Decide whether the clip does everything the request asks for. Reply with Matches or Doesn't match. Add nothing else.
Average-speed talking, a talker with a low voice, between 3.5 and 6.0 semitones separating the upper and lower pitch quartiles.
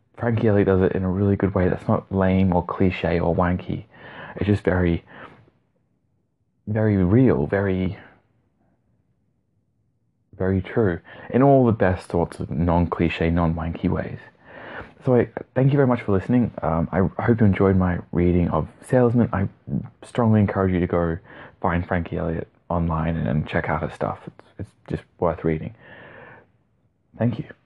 Matches